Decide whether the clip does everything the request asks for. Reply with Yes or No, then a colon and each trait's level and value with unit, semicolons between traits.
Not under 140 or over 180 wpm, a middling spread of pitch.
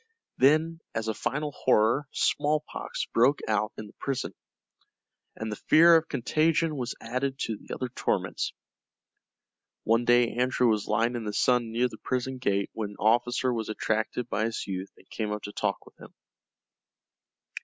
Yes: average, 165 wpm; average, 3.4 semitones